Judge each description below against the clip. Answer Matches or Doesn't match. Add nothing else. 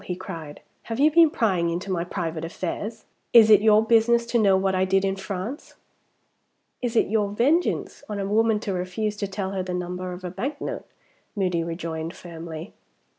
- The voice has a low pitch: Doesn't match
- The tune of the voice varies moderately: Matches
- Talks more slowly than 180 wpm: Doesn't match